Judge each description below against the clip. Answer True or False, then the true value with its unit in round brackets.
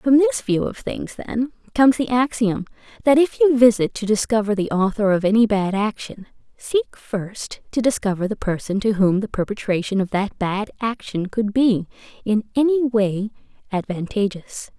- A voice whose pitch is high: True (215 Hz)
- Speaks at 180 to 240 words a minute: False (165 wpm)